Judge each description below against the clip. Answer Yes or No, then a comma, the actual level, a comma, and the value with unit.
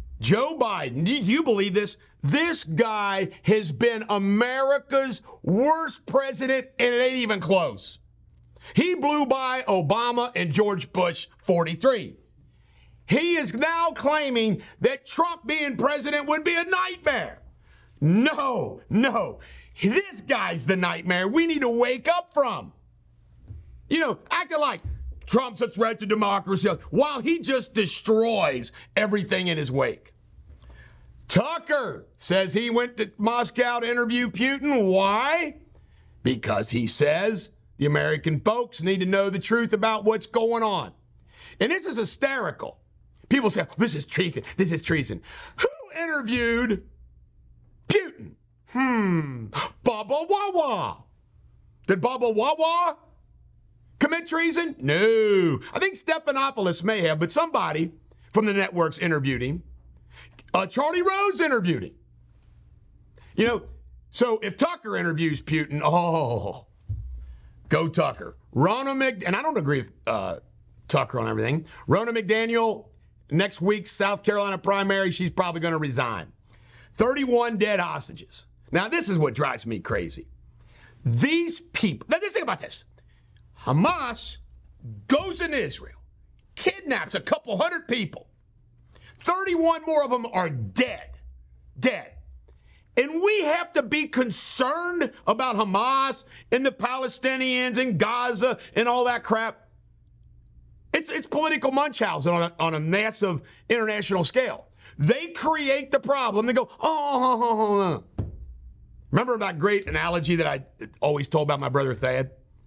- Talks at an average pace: No, slow, 130 wpm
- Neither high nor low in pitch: No, high, 210 Hz